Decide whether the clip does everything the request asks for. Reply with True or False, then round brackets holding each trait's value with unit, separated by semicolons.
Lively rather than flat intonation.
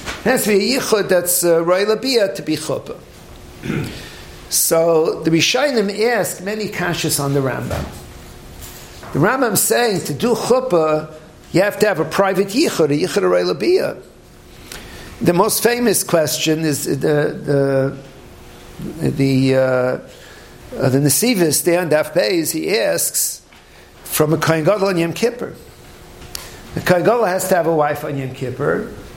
True (6.0 semitones)